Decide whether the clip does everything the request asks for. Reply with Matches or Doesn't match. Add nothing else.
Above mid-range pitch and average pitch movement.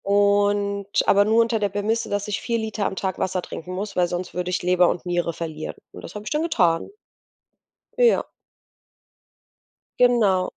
Matches